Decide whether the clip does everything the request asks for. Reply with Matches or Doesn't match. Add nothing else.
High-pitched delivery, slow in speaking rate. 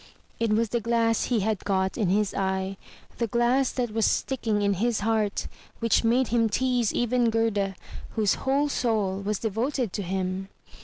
Doesn't match